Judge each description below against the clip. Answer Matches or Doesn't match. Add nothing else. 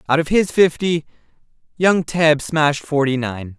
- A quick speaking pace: Doesn't match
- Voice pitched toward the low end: Doesn't match